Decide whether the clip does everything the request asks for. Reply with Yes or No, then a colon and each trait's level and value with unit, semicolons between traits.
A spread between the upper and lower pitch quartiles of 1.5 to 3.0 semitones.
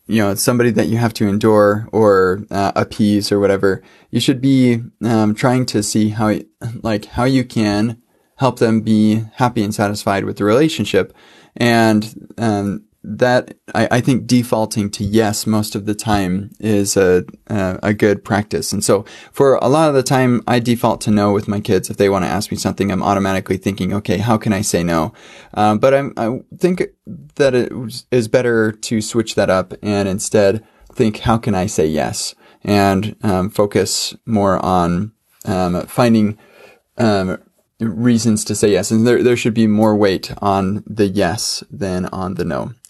Yes: narrow, 2.6 semitones